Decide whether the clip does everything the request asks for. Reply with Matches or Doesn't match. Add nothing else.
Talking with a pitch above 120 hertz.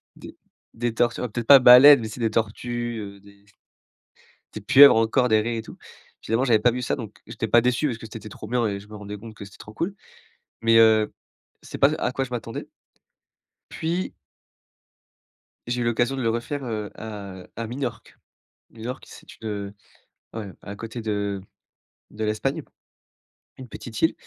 Doesn't match